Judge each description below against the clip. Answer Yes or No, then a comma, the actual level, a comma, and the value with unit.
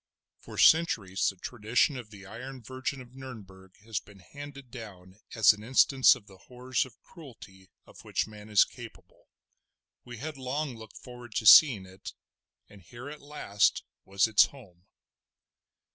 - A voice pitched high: No, low, 115 Hz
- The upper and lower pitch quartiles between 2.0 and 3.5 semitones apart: No, average, 4.6 semitones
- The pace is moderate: Yes, average, 160 wpm